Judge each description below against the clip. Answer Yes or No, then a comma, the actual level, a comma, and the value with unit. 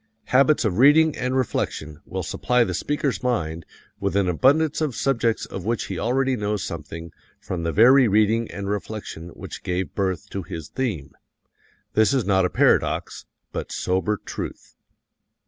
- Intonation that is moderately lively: No, wide, 5.8 semitones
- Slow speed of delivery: No, average, 160 wpm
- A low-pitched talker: Yes, low, 105 Hz